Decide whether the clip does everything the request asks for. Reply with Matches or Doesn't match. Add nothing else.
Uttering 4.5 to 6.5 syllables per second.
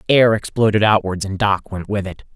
Matches